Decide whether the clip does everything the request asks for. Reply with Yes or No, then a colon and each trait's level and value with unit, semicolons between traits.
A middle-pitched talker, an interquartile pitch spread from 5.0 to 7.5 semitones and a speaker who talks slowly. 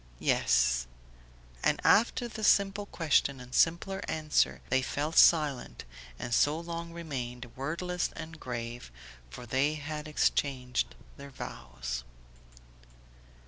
Yes: medium, 145 Hz; average, 5.3 semitones; slow, 110 wpm